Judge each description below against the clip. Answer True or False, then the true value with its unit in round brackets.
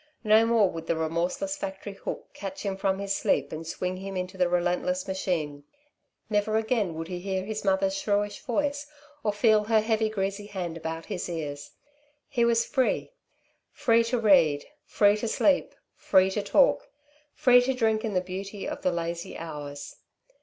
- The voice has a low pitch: False (195 Hz)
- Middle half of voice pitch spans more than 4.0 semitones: False (3.7 semitones)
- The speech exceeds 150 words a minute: True (175 wpm)